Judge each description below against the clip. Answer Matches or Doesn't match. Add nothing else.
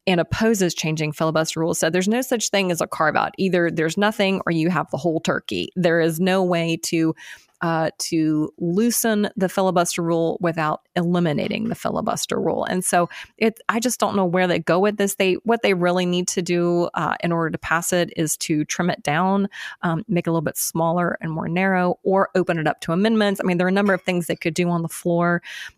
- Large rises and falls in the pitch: Doesn't match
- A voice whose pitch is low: Doesn't match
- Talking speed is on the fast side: Matches